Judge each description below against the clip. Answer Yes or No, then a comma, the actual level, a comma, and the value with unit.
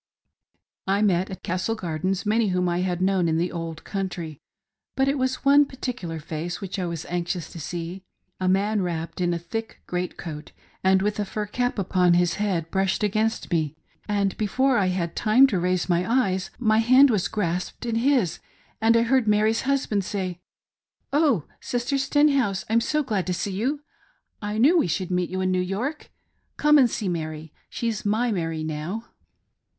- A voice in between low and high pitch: No, high, 195 Hz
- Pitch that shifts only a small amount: No, average, 4.5 semitones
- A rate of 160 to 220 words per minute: Yes, average, 190 wpm